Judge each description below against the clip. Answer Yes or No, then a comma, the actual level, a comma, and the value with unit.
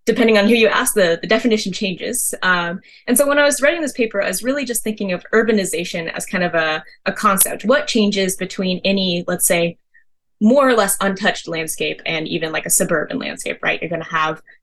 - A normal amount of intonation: Yes, average, 4.5 semitones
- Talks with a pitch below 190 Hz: No, high, 200 Hz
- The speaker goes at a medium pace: No, fast, 215 wpm